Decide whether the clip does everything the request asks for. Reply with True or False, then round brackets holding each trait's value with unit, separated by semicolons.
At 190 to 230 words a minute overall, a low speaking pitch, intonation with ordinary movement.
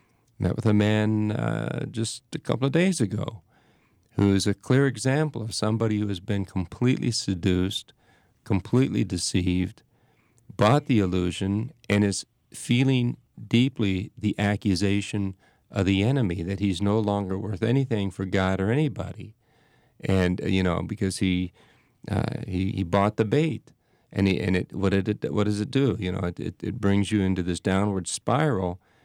False (165 wpm; 105 Hz; 3.5 semitones)